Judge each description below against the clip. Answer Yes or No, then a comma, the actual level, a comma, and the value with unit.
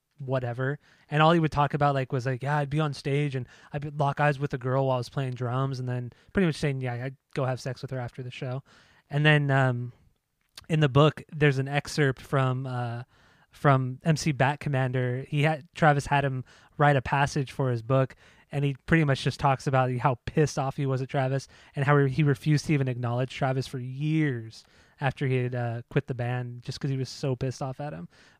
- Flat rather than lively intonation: Yes, narrow, 2.2 semitones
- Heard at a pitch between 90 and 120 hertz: No, low, 135 Hz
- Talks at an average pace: No, fast, 230 wpm